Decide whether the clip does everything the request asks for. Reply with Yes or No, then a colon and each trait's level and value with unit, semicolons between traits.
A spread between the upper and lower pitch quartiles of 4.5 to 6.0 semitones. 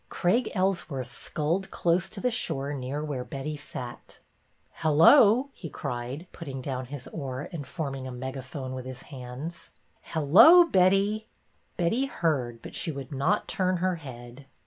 Yes: wide, 5.6 semitones